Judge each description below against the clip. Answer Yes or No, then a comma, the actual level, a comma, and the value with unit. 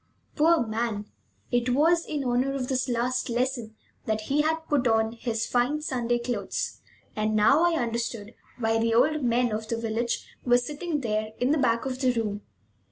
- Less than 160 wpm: No, average, 180 wpm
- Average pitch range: Yes, average, 3.2 semitones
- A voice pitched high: Yes, high, 245 Hz